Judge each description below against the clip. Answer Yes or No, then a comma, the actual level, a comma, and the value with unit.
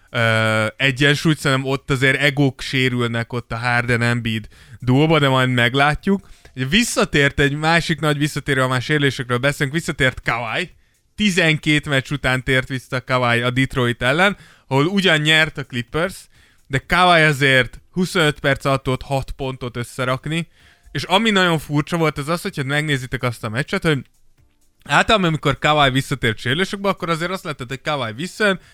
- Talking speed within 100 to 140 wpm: No, fast, 155 wpm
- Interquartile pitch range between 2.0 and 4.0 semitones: Yes, average, 3.6 semitones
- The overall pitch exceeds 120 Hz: Yes, medium, 140 Hz